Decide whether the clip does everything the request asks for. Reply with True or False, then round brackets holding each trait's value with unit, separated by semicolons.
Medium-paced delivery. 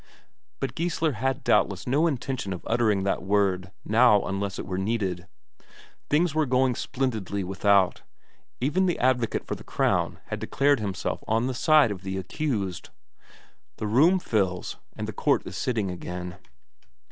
True (155 wpm)